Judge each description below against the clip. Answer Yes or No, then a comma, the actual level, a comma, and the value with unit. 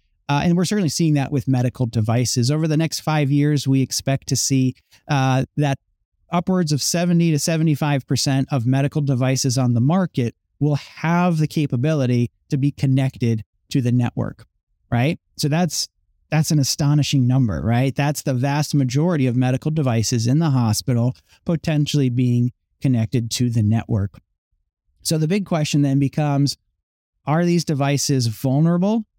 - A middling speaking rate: Yes, average, 155 wpm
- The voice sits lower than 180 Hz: Yes, low, 135 Hz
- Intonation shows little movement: No, average, 3.7 semitones